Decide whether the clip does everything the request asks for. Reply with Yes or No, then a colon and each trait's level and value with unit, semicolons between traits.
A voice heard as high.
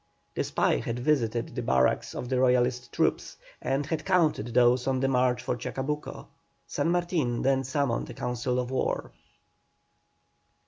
No: low, 130 Hz